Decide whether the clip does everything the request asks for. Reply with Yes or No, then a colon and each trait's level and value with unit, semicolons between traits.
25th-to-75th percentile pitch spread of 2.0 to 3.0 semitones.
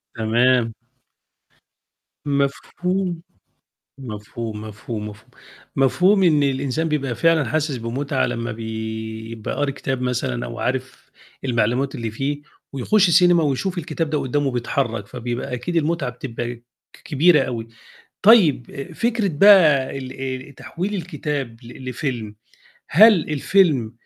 No: average, 5.1 semitones